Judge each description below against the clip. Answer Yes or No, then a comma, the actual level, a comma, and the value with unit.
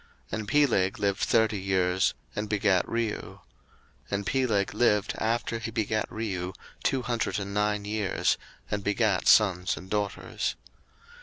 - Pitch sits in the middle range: No, low, 105 Hz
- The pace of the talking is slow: No, average, 145 wpm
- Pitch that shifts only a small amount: Yes, narrow, 2.2 semitones